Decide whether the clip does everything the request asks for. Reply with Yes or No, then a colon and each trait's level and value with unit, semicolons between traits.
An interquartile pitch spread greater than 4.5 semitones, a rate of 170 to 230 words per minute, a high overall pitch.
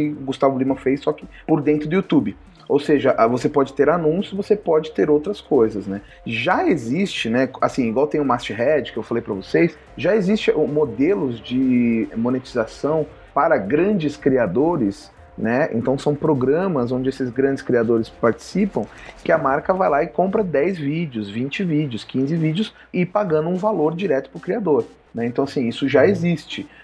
No: average, 5.2 semitones; average, 175 wpm; medium, 150 Hz